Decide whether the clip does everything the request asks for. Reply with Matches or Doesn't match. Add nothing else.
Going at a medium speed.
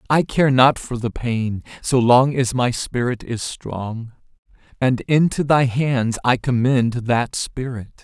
Matches